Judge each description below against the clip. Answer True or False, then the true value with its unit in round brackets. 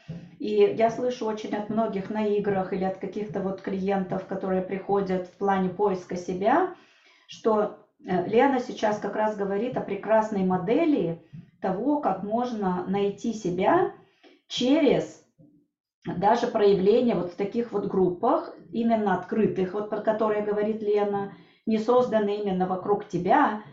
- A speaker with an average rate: True (135 wpm)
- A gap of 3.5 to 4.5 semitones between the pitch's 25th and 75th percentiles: False (2.7 semitones)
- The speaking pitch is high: True (205 Hz)